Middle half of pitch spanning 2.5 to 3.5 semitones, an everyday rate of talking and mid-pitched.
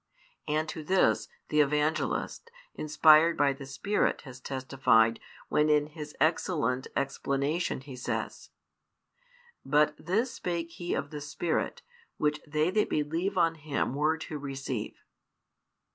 No: average, 2.9 semitones; slow, 130 wpm; medium, 150 Hz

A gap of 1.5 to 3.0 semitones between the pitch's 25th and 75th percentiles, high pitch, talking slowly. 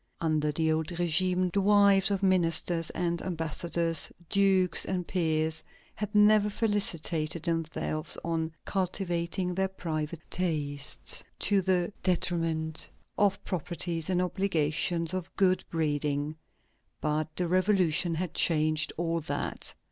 No: average, 2.7 semitones; medium, 170 Hz; slow, 120 wpm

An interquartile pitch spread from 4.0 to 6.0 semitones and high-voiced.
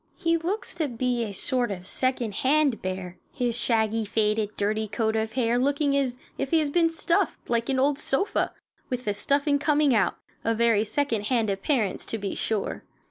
Yes: average, 4.7 semitones; high, 240 Hz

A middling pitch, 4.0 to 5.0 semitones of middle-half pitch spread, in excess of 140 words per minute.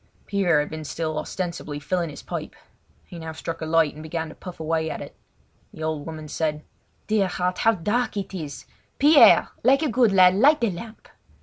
Yes: medium, 170 Hz; average, 4.3 semitones; average, 200 wpm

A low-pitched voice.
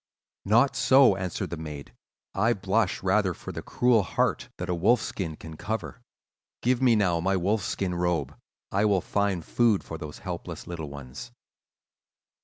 Yes: very low, 95 Hz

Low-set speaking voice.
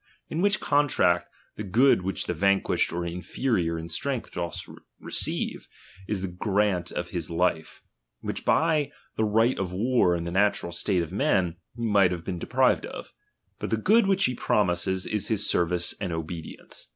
Yes: very low, 95 Hz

